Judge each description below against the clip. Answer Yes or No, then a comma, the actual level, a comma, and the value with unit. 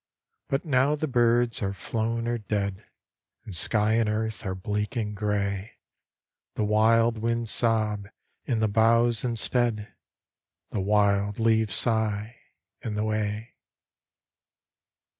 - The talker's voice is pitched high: No, low, 110 Hz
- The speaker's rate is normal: No, slow, 120 wpm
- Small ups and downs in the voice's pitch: Yes, narrow, 2.0 semitones